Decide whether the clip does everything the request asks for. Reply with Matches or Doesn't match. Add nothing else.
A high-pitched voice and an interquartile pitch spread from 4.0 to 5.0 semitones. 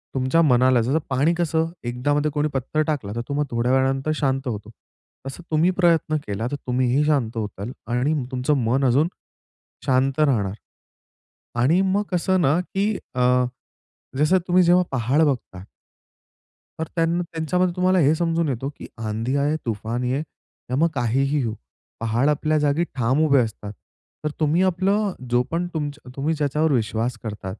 Doesn't match